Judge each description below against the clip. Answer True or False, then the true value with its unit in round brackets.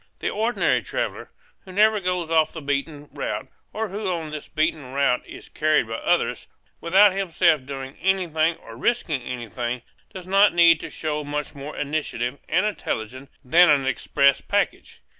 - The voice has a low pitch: False (155 Hz)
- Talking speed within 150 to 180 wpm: True (160 wpm)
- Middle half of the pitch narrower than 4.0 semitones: False (4.7 semitones)